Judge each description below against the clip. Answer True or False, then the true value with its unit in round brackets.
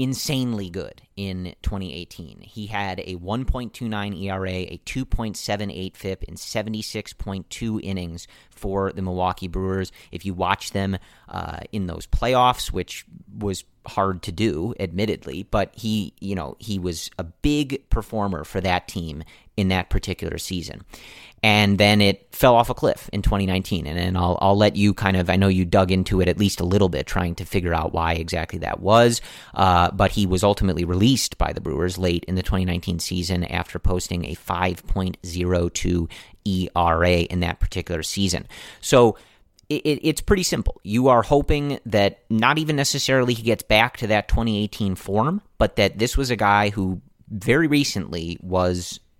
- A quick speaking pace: False (170 wpm)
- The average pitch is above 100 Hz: False (95 Hz)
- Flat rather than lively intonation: False (3.2 semitones)